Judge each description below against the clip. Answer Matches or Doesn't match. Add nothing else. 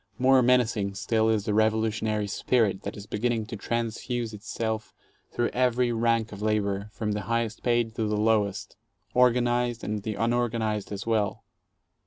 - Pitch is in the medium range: Doesn't match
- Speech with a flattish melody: Matches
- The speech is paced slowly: Doesn't match